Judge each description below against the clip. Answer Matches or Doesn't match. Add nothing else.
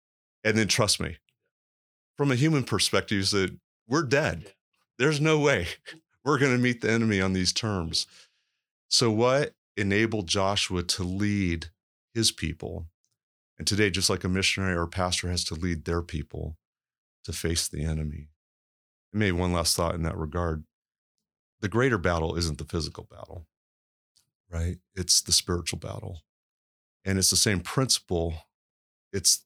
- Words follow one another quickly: Doesn't match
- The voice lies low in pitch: Matches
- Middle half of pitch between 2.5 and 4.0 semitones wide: Doesn't match